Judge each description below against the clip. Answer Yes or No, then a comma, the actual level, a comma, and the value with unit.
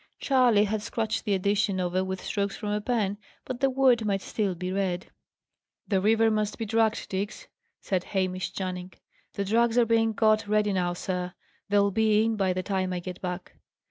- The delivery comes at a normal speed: Yes, average, 190 wpm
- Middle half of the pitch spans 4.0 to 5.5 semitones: No, average, 2.9 semitones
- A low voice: No, high, 205 Hz